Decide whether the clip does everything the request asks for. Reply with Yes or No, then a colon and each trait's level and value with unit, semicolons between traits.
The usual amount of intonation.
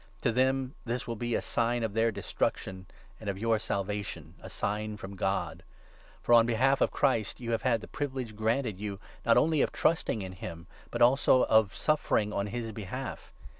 Yes: average, 3.4 semitones